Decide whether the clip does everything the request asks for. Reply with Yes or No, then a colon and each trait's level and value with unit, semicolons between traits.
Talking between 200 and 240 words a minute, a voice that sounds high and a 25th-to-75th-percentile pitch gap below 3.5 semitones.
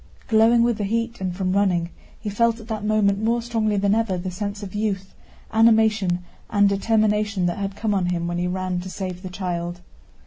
Yes: fast, 205 wpm; high, 200 Hz; average, 3.0 semitones